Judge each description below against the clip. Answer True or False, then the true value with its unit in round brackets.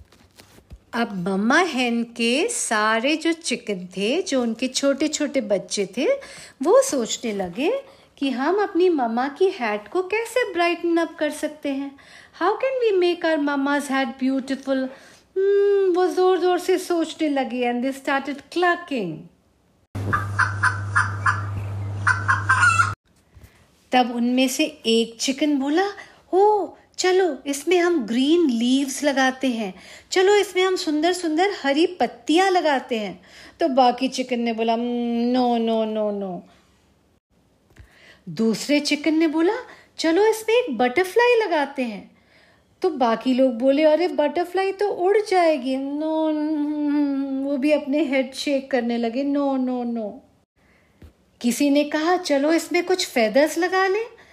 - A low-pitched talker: False (280 Hz)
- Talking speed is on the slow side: False (130 wpm)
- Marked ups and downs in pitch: True (6.5 semitones)